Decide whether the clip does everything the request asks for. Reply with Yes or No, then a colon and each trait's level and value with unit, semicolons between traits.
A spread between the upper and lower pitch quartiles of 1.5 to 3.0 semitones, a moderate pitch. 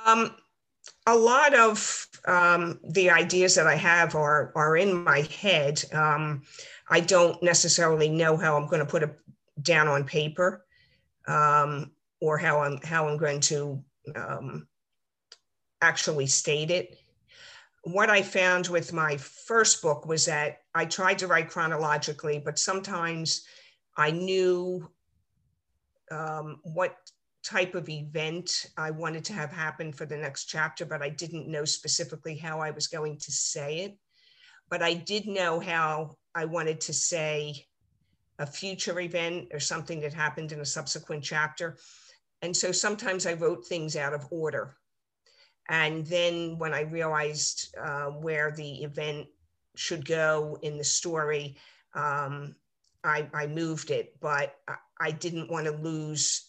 Yes: narrow, 2.6 semitones; medium, 160 Hz